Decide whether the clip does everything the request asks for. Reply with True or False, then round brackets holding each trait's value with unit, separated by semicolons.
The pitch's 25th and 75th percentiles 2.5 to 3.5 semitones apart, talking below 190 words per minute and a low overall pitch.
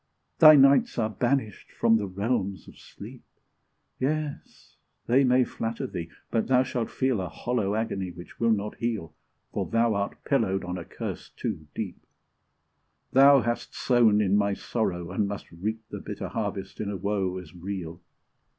False (4.3 semitones; 165 wpm; 110 Hz)